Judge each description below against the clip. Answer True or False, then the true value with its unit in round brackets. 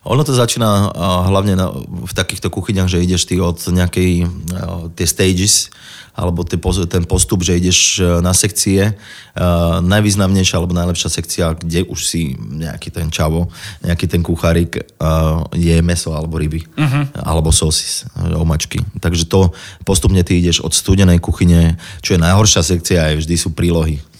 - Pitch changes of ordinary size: False (2.3 semitones)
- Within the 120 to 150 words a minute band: True (140 wpm)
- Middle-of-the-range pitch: False (90 Hz)